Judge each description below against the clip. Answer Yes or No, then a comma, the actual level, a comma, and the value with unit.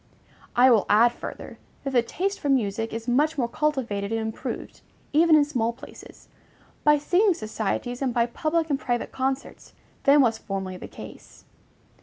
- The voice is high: Yes, very high, 250 Hz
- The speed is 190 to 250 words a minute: No, average, 165 wpm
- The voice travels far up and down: No, average, 4.7 semitones